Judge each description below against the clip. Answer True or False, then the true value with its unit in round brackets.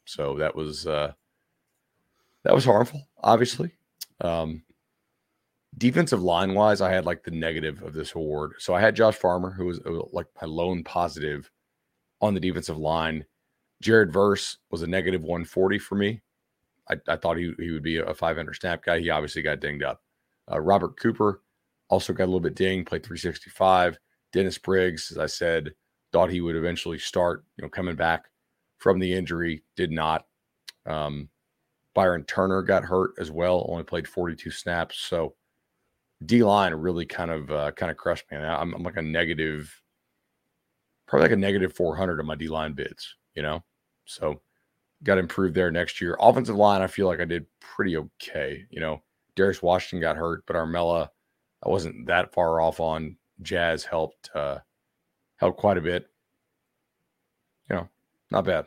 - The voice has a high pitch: False (85 Hz)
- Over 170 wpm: True (180 wpm)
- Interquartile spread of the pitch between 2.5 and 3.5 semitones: True (2.8 semitones)